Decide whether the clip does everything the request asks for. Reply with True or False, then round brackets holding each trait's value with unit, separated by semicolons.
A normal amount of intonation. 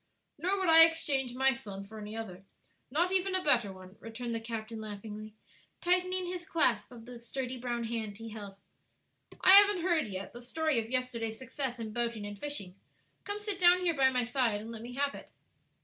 False (6.6 semitones)